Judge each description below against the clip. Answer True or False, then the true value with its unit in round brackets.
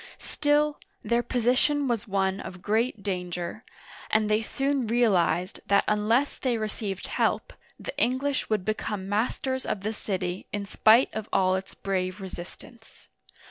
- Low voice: False (215 Hz)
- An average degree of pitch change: True (4.2 semitones)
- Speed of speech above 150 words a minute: False (145 wpm)